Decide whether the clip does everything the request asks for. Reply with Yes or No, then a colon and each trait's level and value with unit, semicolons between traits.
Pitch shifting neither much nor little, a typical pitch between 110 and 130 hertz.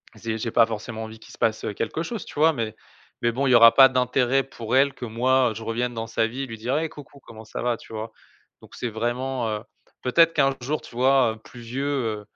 Yes: average, 3.1 semitones; low, 120 Hz